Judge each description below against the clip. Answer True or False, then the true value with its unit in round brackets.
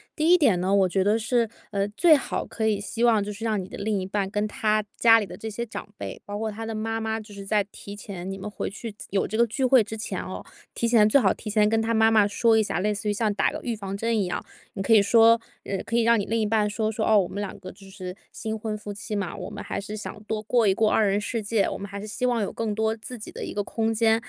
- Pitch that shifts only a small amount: True (1.8 semitones)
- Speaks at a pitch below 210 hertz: False (215 Hz)